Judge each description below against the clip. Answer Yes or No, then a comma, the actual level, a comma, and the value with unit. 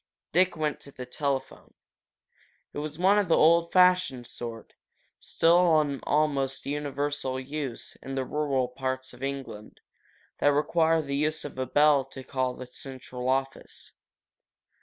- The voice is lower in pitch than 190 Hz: Yes, medium, 140 Hz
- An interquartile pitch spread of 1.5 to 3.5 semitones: Yes, average, 2.8 semitones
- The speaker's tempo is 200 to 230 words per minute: No, average, 145 wpm